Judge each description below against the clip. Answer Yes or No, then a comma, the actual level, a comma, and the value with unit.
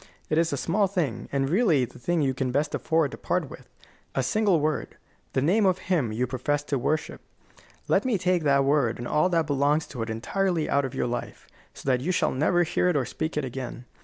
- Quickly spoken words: Yes, fast, 230 wpm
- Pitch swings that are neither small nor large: Yes, average, 4.9 semitones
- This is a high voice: No, medium, 145 Hz